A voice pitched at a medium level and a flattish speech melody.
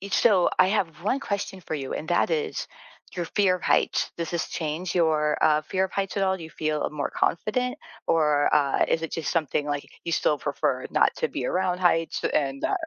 No: medium, 170 Hz; average, 3.9 semitones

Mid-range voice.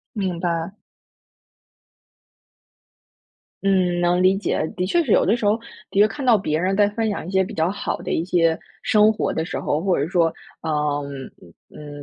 Yes: medium, 180 Hz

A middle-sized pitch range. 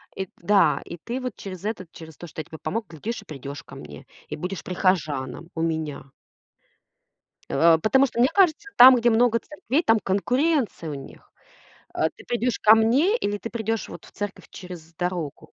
No: wide, 6.6 semitones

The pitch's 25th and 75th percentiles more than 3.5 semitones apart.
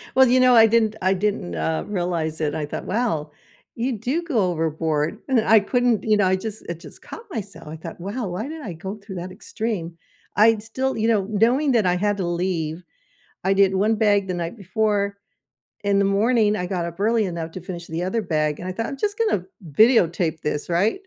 Yes: average, 4.7 semitones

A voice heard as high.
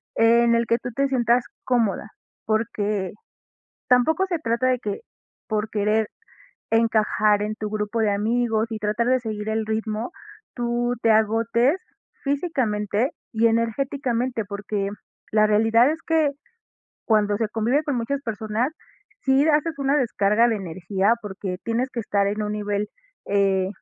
Yes: high, 225 Hz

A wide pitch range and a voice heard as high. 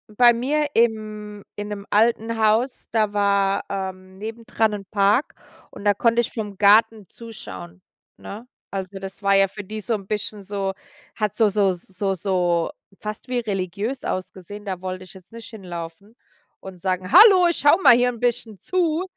No: average, 2.9 semitones; high, 205 Hz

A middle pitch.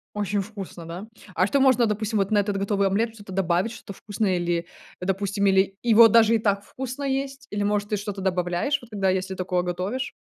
No: high, 200 Hz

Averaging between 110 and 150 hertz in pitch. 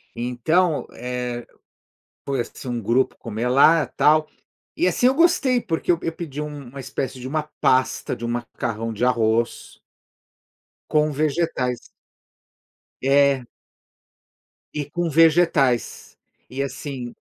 Yes: low, 135 Hz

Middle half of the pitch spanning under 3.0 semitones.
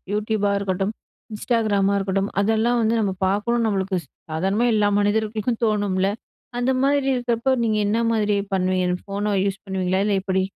Yes: narrow, 2.5 semitones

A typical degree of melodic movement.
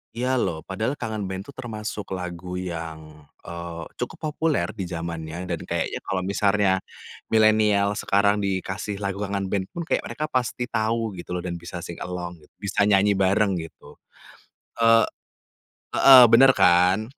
Yes: average, 3.5 semitones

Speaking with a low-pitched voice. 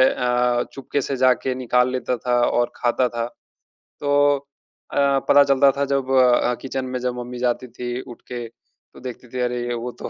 Yes: low, 125 Hz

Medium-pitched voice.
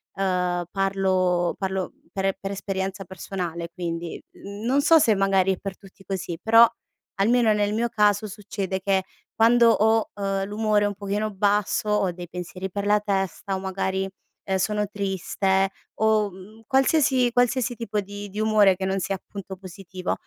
No: high, 195 Hz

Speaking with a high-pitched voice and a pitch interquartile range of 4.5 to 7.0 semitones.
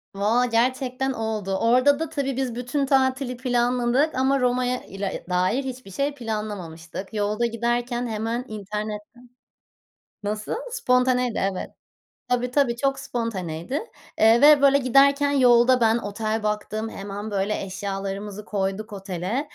No: high, 235 Hz; average, 3.7 semitones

